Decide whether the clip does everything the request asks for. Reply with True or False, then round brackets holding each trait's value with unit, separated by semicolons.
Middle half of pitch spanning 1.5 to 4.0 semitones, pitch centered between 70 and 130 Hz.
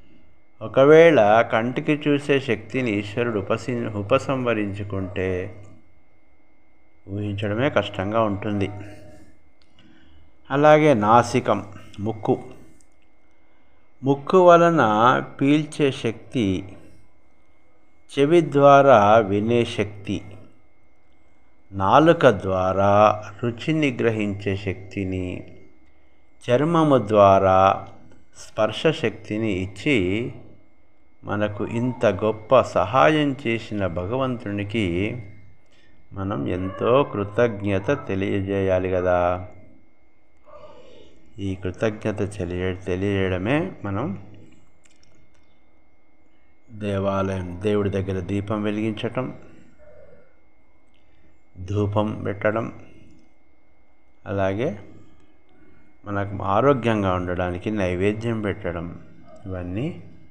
True (3.5 semitones; 105 Hz)